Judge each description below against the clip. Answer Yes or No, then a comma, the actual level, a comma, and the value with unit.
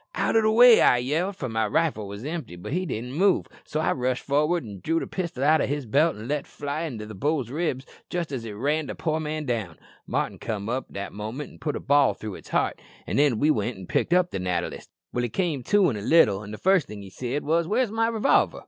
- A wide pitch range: Yes, wide, 6.9 semitones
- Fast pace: Yes, fast, 255 wpm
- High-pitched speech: No, medium, 140 Hz